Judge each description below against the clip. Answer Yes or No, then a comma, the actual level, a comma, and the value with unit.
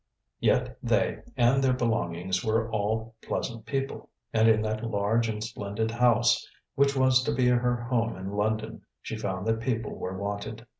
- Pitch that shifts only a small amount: Yes, narrow, 2.1 semitones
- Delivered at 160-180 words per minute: Yes, average, 165 wpm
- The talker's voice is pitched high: No, low, 115 Hz